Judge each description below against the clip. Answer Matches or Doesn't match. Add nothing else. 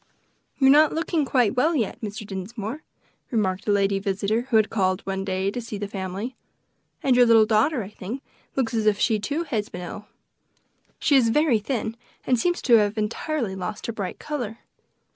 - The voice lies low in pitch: Doesn't match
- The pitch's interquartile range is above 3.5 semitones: Matches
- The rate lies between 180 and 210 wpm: Matches